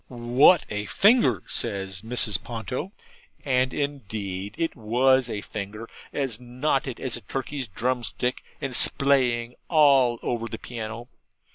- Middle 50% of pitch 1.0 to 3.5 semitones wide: Yes, average, 3.2 semitones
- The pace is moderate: No, slow, 125 wpm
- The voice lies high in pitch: No, low, 120 Hz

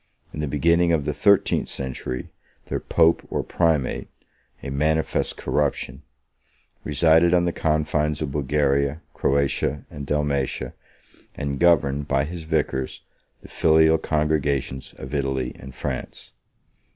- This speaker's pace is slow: Yes, slow, 125 wpm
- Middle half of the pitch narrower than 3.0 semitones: Yes, narrow, 2.6 semitones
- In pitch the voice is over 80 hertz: No, very low, 75 Hz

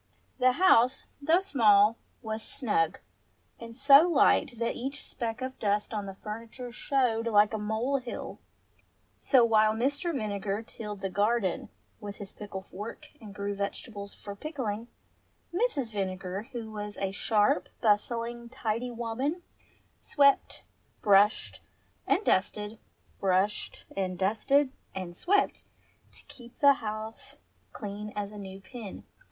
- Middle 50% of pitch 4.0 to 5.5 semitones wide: No, average, 3.6 semitones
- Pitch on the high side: Yes, high, 220 Hz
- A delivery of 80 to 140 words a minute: Yes, slow, 135 wpm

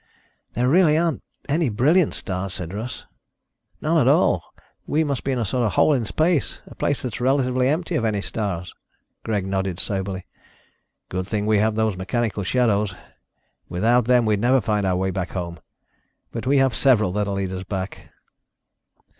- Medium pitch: No, low, 110 Hz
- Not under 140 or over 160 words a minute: No, average, 180 wpm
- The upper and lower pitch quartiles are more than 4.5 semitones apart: Yes, average, 5.0 semitones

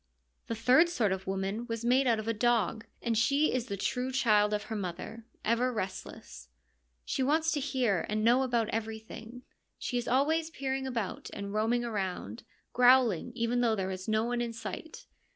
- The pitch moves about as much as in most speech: Yes, average, 3.0 semitones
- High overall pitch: Yes, high, 230 Hz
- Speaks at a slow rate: No, average, 185 wpm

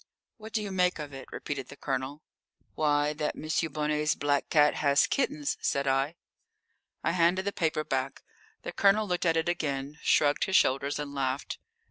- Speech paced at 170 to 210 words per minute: Yes, average, 175 wpm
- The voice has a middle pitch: Yes, medium, 150 Hz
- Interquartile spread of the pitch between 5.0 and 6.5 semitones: No, average, 3.3 semitones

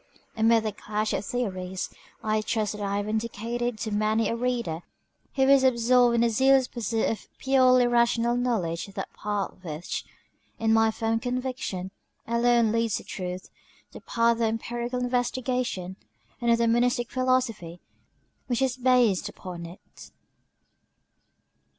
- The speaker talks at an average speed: Yes, average, 150 wpm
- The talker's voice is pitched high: Yes, high, 230 Hz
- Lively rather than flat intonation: No, average, 2.8 semitones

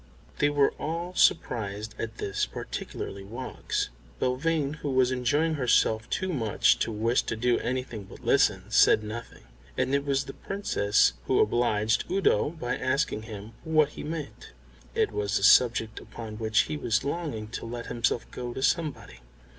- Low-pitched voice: Yes, low, 120 Hz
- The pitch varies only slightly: No, average, 4.8 semitones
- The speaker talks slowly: No, average, 160 wpm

